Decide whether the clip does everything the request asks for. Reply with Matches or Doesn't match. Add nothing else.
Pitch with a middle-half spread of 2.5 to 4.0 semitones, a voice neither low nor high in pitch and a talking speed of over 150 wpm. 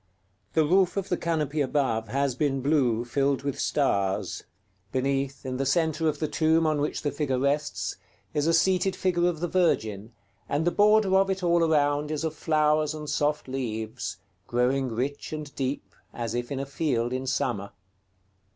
Matches